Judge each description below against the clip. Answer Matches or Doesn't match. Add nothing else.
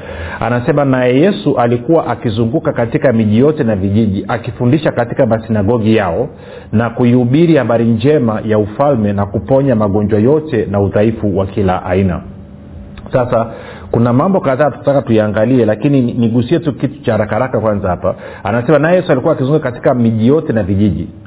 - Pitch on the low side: Matches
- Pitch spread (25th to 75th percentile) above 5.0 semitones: Doesn't match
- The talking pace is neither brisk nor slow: Doesn't match